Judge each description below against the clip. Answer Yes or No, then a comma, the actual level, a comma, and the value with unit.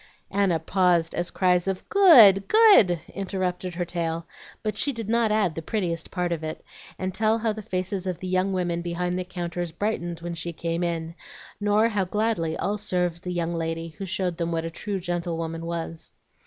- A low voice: No, medium, 180 Hz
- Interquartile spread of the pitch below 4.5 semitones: Yes, average, 2.9 semitones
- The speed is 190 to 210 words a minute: Yes, average, 195 wpm